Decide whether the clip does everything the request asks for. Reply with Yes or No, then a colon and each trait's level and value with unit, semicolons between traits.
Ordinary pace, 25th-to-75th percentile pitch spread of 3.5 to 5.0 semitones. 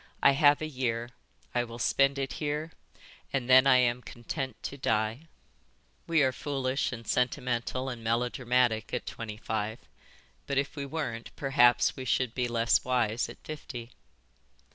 No: average, 155 wpm; average, 2.7 semitones